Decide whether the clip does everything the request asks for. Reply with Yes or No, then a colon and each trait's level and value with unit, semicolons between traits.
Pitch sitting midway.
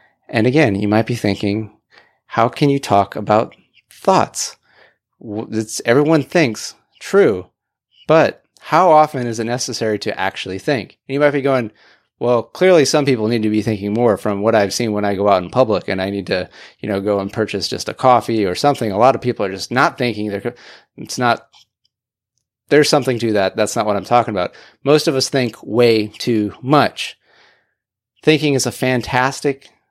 No: low, 115 Hz